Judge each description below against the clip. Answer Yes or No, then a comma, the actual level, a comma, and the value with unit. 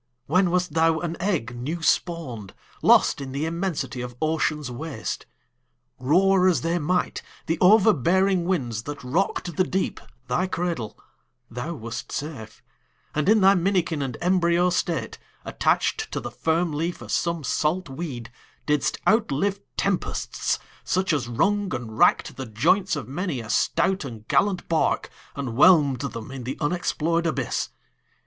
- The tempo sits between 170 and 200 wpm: No, average, 150 wpm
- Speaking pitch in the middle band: Yes, medium, 165 Hz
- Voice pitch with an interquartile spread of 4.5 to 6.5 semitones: Yes, average, 5.3 semitones